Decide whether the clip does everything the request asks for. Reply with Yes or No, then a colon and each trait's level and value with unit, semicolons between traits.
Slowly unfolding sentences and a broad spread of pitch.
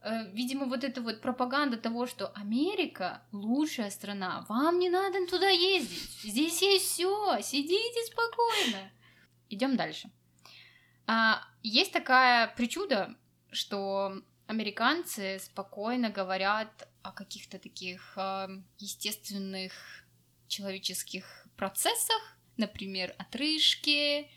Yes: slow, 90 wpm; wide, 7.5 semitones